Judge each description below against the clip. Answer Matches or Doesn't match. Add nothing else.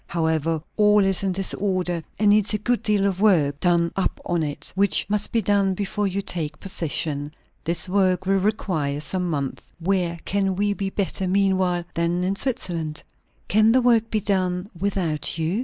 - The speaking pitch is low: Doesn't match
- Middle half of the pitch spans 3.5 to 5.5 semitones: Doesn't match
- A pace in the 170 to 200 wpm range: Matches